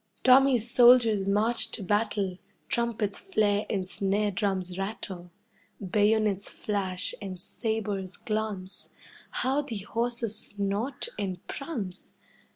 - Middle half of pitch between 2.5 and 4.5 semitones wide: Yes, average, 3.0 semitones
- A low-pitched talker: No, high, 205 Hz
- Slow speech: Yes, slow, 105 wpm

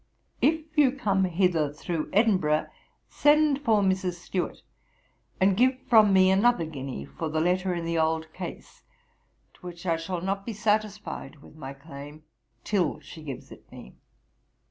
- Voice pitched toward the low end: No, medium, 180 Hz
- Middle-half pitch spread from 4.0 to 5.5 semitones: Yes, average, 4.7 semitones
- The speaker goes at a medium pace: Yes, average, 155 wpm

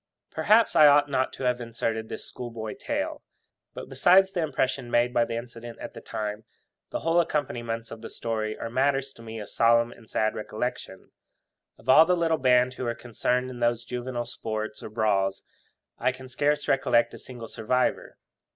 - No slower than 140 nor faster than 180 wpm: No, average, 190 wpm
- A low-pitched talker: Yes, low, 120 Hz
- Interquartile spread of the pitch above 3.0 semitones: No, narrow, 2.6 semitones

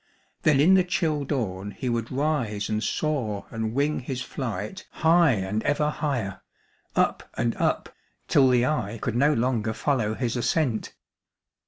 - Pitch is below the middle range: Yes, low, 125 Hz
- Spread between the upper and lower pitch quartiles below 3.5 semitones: No, average, 5.3 semitones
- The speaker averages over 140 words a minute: Yes, average, 155 wpm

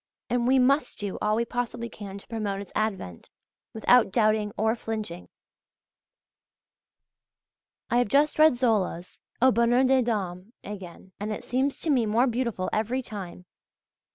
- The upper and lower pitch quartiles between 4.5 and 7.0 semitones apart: No, average, 3.4 semitones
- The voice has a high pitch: Yes, high, 225 Hz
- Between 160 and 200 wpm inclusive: No, average, 150 wpm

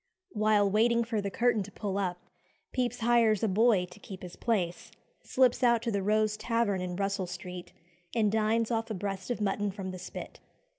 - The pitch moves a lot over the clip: No, average, 3.1 semitones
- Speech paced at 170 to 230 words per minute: Yes, average, 195 wpm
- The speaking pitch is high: Yes, high, 210 Hz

